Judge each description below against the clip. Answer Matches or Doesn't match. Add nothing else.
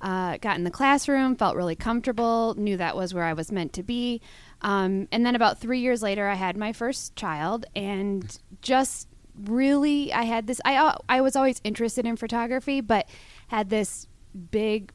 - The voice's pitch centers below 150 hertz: Doesn't match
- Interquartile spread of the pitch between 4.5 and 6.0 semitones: Doesn't match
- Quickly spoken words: Doesn't match